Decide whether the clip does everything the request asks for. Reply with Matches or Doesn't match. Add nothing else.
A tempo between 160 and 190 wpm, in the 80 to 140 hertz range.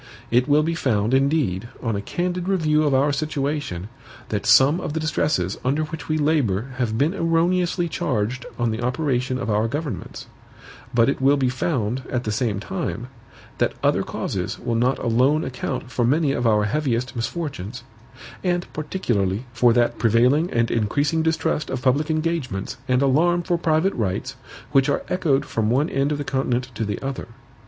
Matches